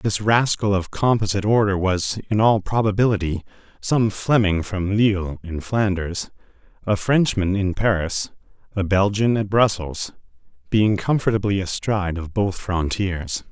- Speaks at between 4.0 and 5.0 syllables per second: Yes, 4.5 syllables/s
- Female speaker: No, male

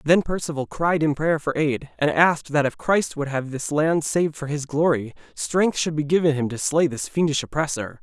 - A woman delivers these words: No, male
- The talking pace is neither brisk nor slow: No, fast, 225 wpm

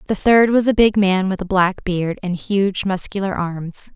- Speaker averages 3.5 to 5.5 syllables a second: Yes, 4.3 syllables/s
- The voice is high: Yes, high, 195 Hz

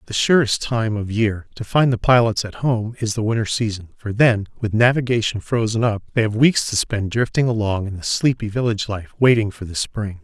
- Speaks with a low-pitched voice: Yes, low, 110 Hz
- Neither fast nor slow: No, fast, 215 wpm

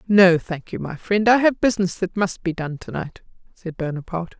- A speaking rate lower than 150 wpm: No, fast, 205 wpm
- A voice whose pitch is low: No, medium, 185 Hz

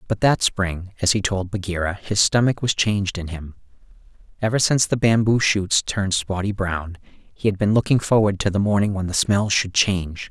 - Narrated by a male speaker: Yes, male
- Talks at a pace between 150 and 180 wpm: No, average, 200 wpm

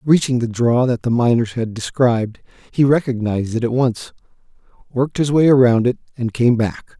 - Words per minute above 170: Yes, average, 180 wpm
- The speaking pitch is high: No, low, 120 Hz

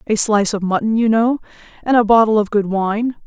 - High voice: Yes, high, 215 Hz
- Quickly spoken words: Yes, fast, 220 wpm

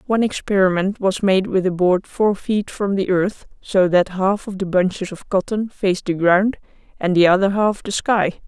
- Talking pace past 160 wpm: Yes, fast, 205 wpm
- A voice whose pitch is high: Yes, high, 195 Hz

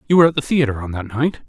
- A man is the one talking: Yes, male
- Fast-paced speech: Yes, fast, 325 wpm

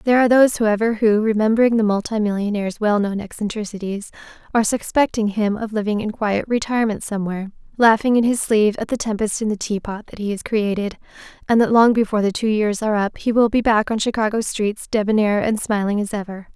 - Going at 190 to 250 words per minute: Yes, average, 200 wpm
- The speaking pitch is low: No, high, 215 Hz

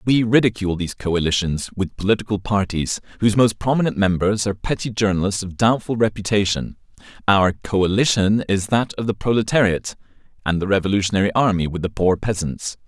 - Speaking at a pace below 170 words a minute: Yes, average, 150 wpm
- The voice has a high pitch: No, low, 100 Hz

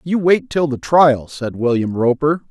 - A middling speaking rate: Yes, average, 190 wpm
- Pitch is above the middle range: No, medium, 145 Hz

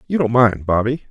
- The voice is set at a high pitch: No, low, 120 Hz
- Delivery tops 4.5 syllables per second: Yes, 5.4 syllables/s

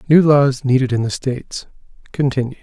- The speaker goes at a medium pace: Yes, average, 160 wpm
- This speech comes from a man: Yes, male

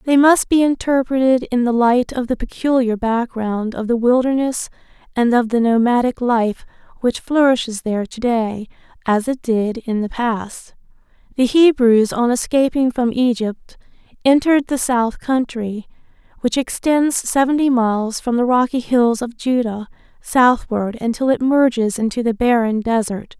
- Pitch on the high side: Yes, high, 240 Hz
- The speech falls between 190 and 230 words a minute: No, average, 150 wpm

